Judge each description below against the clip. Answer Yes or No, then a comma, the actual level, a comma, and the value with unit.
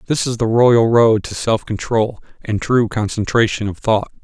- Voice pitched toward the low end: Yes, low, 115 Hz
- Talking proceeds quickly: No, average, 185 wpm